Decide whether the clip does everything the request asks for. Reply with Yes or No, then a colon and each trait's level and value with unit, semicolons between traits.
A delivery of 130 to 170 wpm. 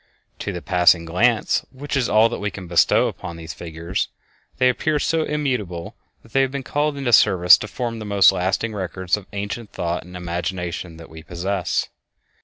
No: average, 190 wpm